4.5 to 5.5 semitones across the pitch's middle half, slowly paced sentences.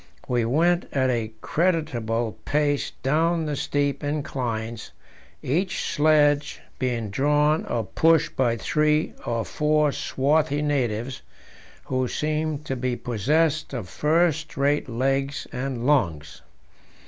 No: average, 3.8 semitones; slow, 115 wpm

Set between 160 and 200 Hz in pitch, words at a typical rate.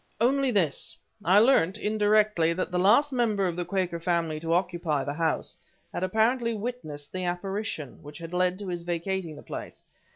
Yes: medium, 185 Hz; average, 175 wpm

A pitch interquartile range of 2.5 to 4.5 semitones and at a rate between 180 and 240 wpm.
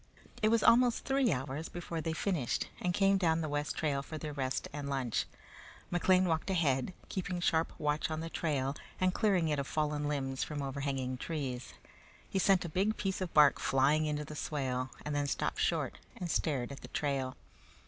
Yes: average, 4.1 semitones; average, 190 wpm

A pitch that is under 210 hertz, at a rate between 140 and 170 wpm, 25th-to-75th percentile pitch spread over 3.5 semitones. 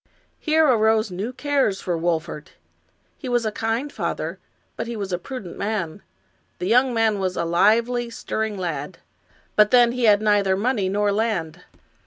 No: high, 215 Hz; average, 165 wpm; average, 4.0 semitones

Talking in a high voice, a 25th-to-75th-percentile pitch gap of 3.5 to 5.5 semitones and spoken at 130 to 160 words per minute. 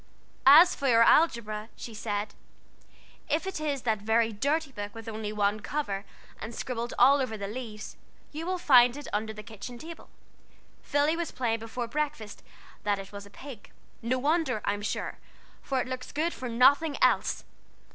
No: high, 235 Hz; average, 5.1 semitones; average, 175 wpm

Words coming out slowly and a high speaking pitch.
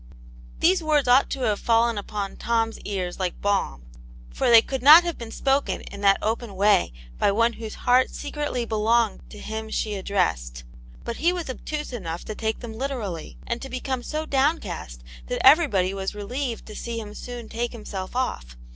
No: average, 180 wpm; high, 230 Hz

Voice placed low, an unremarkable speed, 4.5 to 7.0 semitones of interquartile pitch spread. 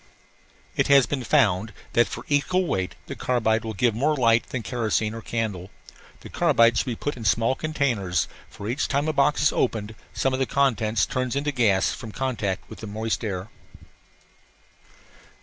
No: low, 115 Hz; average, 180 wpm; average, 3.7 semitones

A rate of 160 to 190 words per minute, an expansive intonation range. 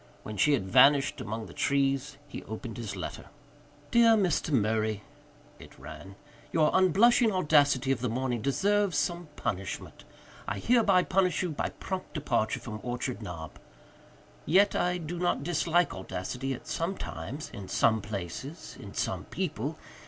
No: average, 150 wpm; wide, 8.1 semitones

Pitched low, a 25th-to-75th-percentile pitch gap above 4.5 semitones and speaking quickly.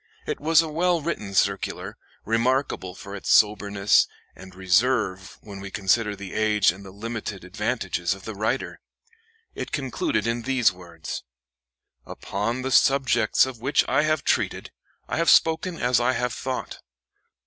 No: low, 110 Hz; average, 5.1 semitones; average, 150 wpm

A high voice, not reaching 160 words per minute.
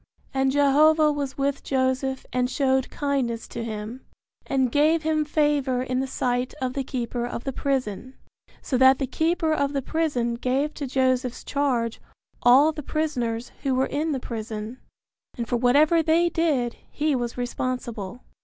No: very high, 265 Hz; average, 165 wpm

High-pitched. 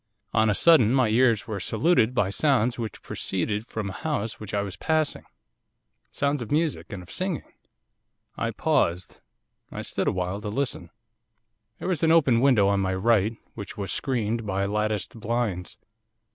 No: low, 110 Hz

